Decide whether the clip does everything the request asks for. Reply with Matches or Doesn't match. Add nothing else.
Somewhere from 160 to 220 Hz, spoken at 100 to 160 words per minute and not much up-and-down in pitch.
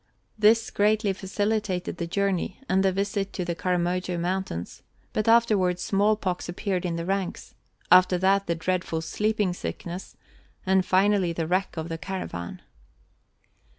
Matches